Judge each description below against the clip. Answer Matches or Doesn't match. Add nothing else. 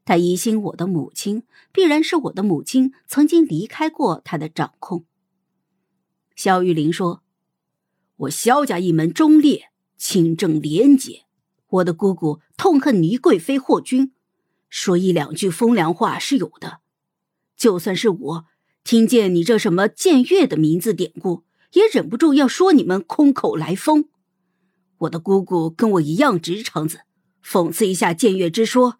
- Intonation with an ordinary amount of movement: Doesn't match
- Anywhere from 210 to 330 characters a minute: Matches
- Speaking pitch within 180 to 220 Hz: Matches